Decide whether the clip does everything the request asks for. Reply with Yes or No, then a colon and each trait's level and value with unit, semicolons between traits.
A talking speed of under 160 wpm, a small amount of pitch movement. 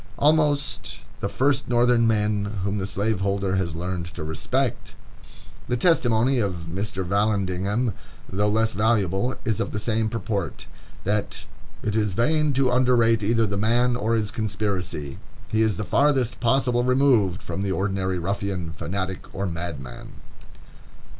No: average, 140 wpm; average, 3.9 semitones